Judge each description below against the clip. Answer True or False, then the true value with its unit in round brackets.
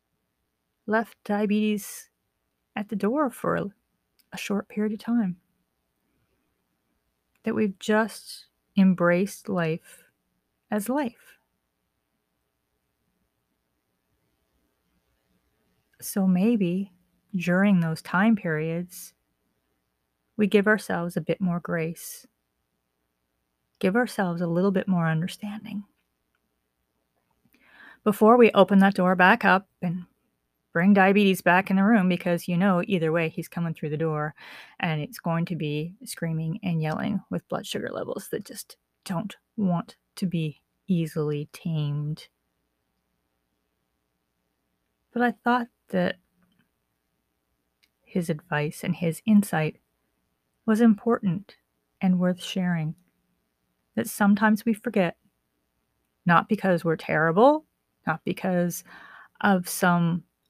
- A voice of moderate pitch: True (170 Hz)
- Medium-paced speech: False (105 wpm)